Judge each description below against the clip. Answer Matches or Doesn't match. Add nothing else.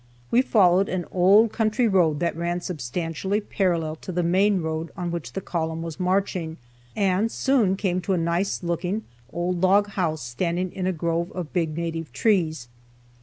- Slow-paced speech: Doesn't match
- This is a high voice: Doesn't match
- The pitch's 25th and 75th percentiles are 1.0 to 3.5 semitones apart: Matches